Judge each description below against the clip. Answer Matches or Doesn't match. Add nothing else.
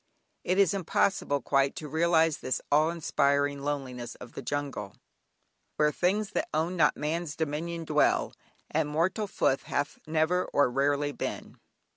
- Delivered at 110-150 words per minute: Matches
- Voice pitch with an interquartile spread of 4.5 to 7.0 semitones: Doesn't match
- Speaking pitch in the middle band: Matches